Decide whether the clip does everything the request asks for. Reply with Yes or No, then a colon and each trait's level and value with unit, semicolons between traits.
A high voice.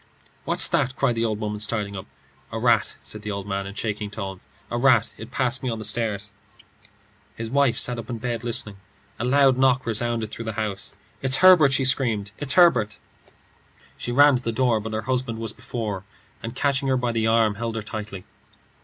No: low, 115 Hz